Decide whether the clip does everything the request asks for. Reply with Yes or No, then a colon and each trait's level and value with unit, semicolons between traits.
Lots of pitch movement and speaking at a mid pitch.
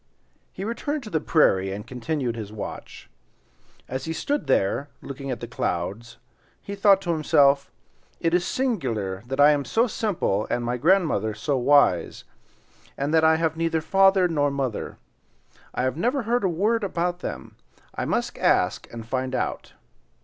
Yes: wide, 7.4 semitones; medium, 145 Hz